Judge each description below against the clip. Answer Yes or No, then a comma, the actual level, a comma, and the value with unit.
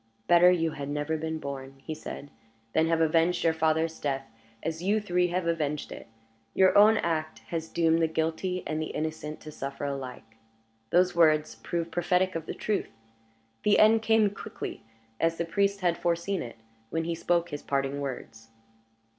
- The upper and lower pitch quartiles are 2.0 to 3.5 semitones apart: Yes, average, 2.7 semitones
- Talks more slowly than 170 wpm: No, average, 175 wpm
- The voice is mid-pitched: Yes, medium, 165 Hz